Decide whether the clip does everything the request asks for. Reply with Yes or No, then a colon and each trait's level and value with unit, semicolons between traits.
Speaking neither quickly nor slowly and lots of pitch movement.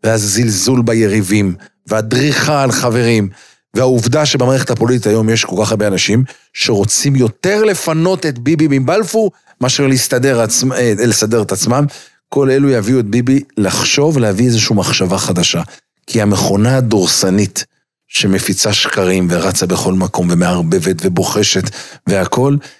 No: average, 120 wpm; average, 4.5 semitones